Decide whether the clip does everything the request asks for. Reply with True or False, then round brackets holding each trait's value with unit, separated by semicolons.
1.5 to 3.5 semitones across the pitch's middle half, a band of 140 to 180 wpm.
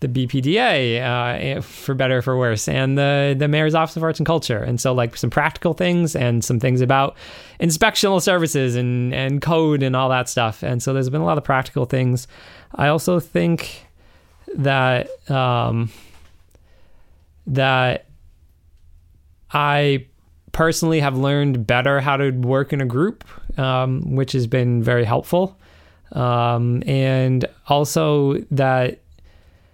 True (3.2 semitones; 145 wpm)